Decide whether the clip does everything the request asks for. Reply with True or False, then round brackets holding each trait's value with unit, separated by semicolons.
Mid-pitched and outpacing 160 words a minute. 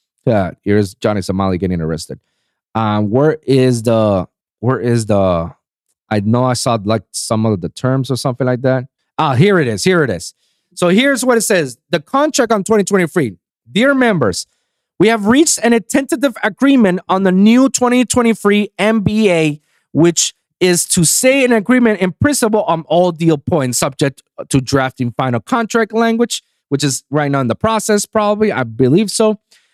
True (170 Hz; 170 wpm)